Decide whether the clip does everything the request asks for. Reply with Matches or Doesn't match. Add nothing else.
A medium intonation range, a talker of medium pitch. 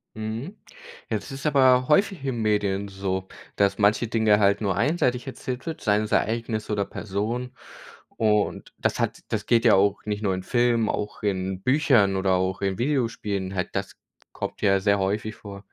Doesn't match